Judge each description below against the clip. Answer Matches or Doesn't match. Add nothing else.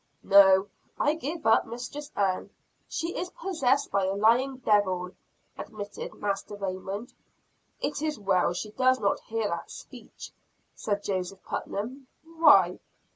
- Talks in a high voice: Matches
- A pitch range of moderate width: Doesn't match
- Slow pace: Matches